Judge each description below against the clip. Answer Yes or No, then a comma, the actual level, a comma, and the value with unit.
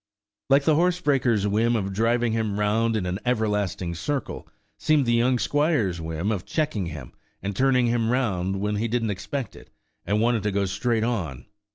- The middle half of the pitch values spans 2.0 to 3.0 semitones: No, average, 3.9 semitones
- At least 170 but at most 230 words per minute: Yes, average, 180 wpm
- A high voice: No, low, 110 Hz